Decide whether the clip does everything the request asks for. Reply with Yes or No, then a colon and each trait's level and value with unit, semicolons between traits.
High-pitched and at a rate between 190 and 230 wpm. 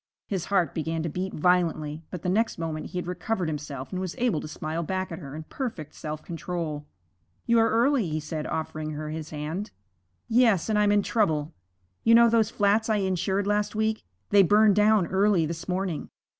No: medium, 180 Hz; average, 200 wpm